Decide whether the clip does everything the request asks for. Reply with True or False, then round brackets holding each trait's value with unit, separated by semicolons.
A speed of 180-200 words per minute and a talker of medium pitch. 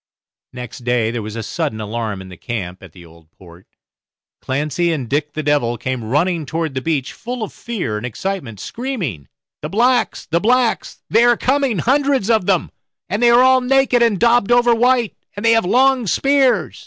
True (190 wpm; 170 Hz)